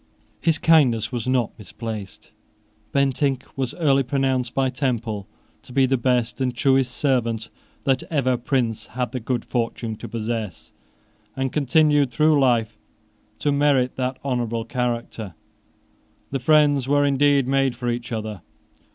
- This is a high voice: No, low, 130 Hz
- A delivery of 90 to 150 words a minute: Yes, average, 140 wpm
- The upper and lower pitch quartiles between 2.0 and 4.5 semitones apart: Yes, average, 2.7 semitones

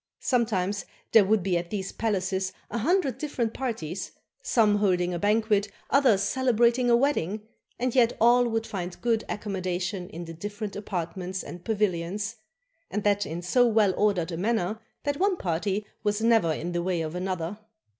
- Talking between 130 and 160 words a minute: No, average, 170 wpm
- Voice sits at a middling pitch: No, high, 205 Hz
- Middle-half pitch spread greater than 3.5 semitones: Yes, average, 4.1 semitones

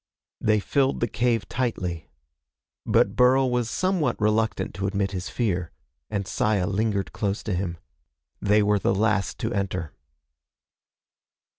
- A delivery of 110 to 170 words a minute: Yes, slow, 135 wpm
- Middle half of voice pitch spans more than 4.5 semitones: No, average, 3.0 semitones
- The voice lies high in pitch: No, low, 105 Hz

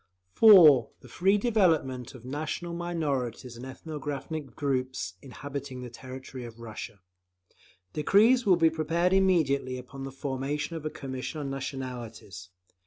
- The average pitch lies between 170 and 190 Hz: No, medium, 140 Hz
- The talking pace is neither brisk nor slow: No, slow, 130 wpm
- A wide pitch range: No, average, 4.2 semitones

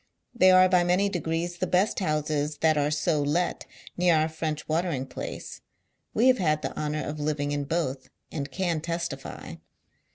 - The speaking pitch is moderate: Yes, medium, 160 Hz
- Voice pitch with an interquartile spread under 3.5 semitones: Yes, average, 3.0 semitones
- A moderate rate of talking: Yes, average, 170 wpm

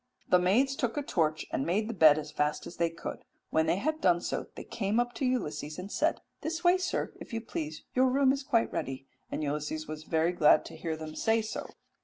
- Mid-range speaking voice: Yes, medium, 180 Hz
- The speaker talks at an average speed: No, fast, 235 wpm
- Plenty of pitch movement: Yes, wide, 8.0 semitones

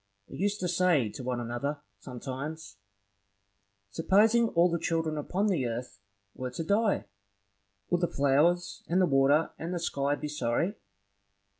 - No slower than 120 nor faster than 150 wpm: Yes, average, 145 wpm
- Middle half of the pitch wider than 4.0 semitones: Yes, average, 4.8 semitones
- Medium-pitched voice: Yes, medium, 155 Hz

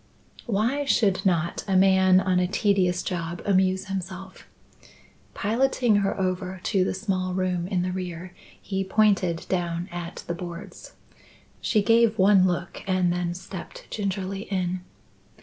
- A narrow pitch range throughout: Yes, narrow, 1.7 semitones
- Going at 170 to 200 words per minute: No, average, 140 wpm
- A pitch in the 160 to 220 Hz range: Yes, medium, 185 Hz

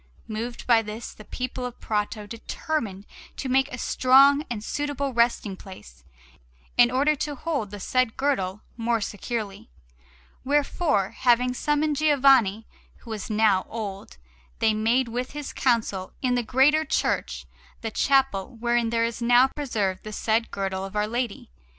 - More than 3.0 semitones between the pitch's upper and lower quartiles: Yes, average, 3.9 semitones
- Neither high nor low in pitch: No, high, 235 Hz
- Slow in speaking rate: No, average, 150 wpm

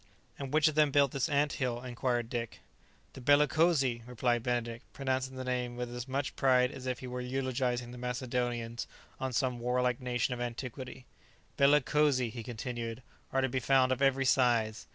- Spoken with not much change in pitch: Yes, narrow, 1.7 semitones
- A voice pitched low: Yes, low, 125 Hz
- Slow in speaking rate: No, average, 175 wpm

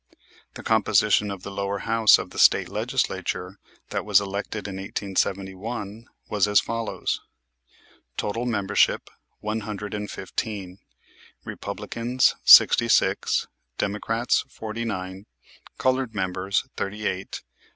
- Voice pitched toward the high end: No, low, 105 Hz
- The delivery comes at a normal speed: No, slow, 115 wpm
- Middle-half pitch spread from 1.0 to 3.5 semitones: Yes, narrow, 2.5 semitones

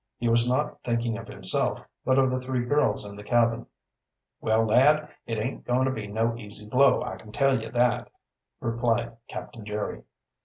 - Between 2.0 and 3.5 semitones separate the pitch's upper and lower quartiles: Yes, narrow, 2.5 semitones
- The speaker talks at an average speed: Yes, average, 185 wpm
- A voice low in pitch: Yes, low, 120 Hz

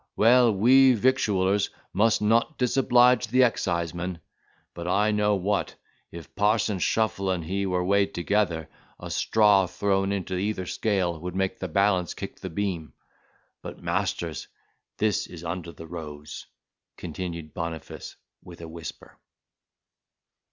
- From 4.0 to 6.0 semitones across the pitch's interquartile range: No, average, 3.6 semitones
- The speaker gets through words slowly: Yes, slow, 130 wpm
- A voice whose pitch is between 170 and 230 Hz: No, very low, 95 Hz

